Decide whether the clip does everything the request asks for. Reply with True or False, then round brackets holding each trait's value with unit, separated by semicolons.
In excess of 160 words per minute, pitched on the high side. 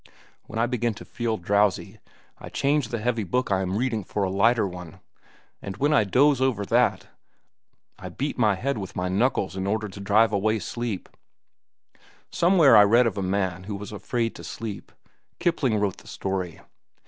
False (185 wpm; 105 Hz)